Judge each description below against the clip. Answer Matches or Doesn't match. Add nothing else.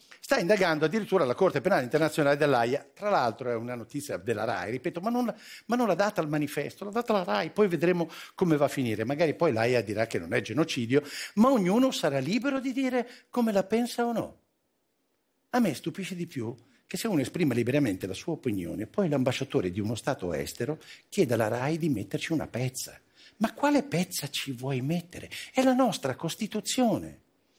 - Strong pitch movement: Matches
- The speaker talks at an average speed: Doesn't match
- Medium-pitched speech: Matches